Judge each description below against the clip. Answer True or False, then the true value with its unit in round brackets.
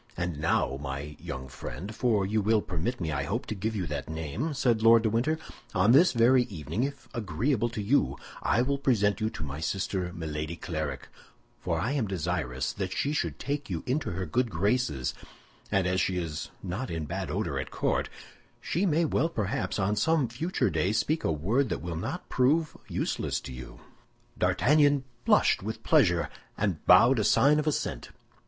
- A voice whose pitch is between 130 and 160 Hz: False (105 Hz)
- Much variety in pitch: True (7.8 semitones)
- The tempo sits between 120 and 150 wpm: False (185 wpm)